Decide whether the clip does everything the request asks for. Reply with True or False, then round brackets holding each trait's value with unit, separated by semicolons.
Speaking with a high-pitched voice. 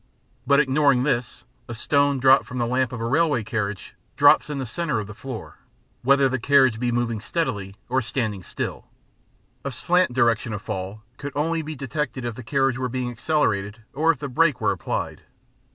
False (130 Hz)